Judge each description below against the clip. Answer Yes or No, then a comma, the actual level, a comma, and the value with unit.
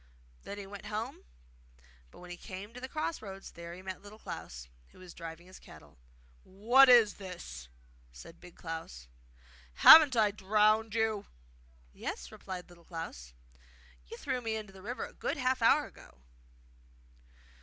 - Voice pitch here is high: Yes, high, 195 Hz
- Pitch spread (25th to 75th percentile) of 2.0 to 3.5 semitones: No, average, 4.4 semitones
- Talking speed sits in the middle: Yes, average, 155 wpm